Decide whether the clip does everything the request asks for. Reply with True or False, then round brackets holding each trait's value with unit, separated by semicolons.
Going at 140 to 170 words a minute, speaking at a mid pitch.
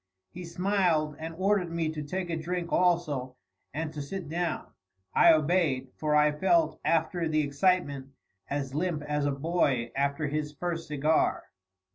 True (155 wpm; 155 Hz)